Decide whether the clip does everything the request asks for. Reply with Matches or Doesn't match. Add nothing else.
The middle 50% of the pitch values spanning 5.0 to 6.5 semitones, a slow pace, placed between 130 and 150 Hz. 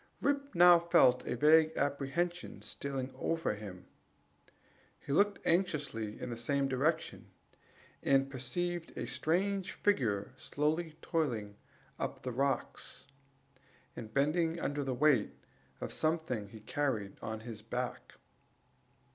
Matches